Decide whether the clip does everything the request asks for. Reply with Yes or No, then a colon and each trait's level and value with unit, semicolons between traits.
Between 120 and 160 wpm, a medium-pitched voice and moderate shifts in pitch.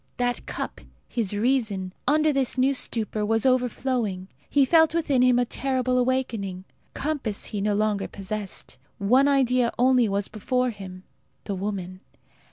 No: average, 145 wpm; high, 240 Hz; average, 4.3 semitones